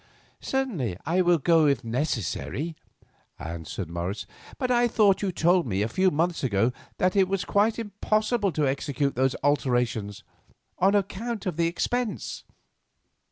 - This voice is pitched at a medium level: Yes, medium, 165 Hz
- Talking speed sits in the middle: Yes, average, 145 wpm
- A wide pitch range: Yes, wide, 8.3 semitones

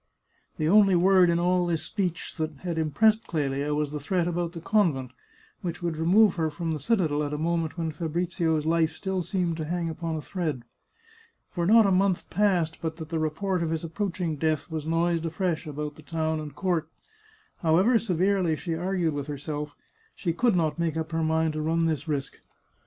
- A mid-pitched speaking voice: Yes, medium, 165 Hz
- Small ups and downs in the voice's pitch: Yes, narrow, 2.3 semitones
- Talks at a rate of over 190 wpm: Yes, average, 200 wpm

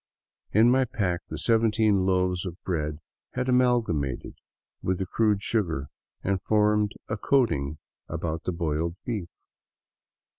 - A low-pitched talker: Yes, very low, 95 Hz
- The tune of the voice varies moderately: Yes, average, 4.8 semitones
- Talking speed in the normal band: No, slow, 125 wpm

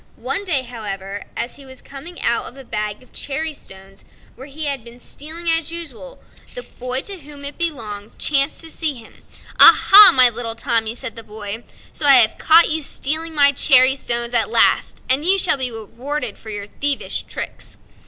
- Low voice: No, very high, 270 Hz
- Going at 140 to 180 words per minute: No, average, 195 wpm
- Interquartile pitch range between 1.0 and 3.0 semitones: No, average, 5.0 semitones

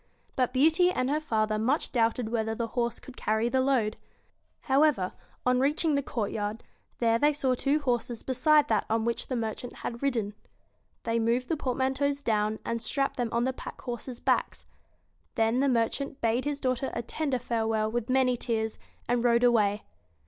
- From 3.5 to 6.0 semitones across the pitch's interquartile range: No, average, 2.9 semitones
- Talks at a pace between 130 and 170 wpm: No, average, 180 wpm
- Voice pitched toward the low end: No, high, 245 Hz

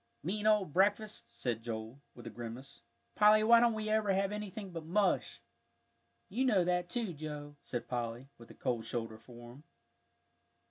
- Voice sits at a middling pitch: Yes, medium, 175 Hz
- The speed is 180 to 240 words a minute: No, average, 170 wpm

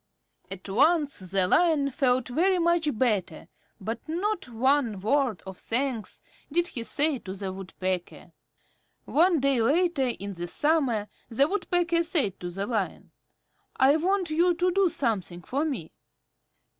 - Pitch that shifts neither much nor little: No, wide, 8.4 semitones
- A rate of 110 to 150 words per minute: Yes, average, 145 wpm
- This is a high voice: Yes, very high, 270 Hz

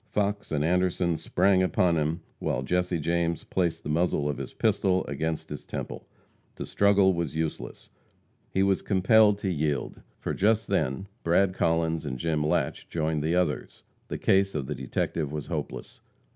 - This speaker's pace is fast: No, average, 165 wpm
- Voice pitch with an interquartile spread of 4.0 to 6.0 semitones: No, average, 3.6 semitones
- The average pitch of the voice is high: No, very low, 85 Hz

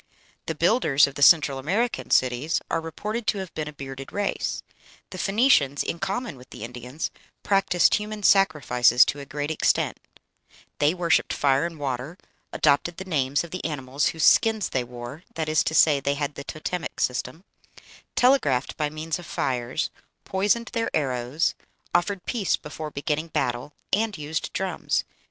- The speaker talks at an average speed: Yes, average, 165 wpm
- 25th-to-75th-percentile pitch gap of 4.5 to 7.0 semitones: Yes, average, 5.3 semitones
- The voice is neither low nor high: Yes, medium, 155 Hz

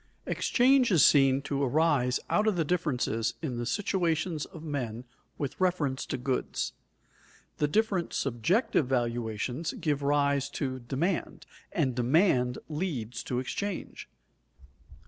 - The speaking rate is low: Yes, slow, 125 wpm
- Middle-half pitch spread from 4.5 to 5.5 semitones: Yes, average, 5.2 semitones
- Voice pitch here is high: No, medium, 140 Hz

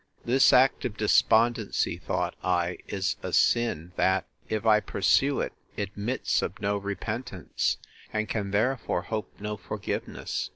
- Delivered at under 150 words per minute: Yes, slow, 135 wpm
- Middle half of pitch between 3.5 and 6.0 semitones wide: No, average, 3.0 semitones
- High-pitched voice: No, low, 105 Hz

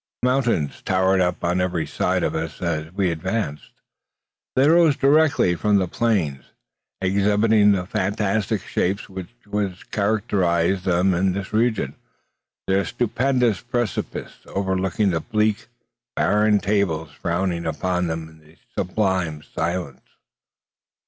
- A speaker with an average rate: No, slow, 115 wpm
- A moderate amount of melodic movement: Yes, average, 3.8 semitones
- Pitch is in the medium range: No, very low, 95 Hz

